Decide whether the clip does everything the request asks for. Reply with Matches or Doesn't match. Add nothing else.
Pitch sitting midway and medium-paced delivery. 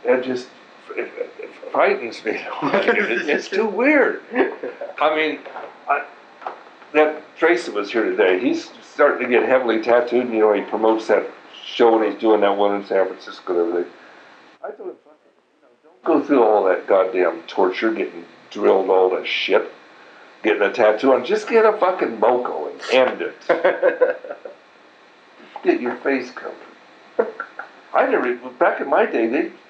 Matches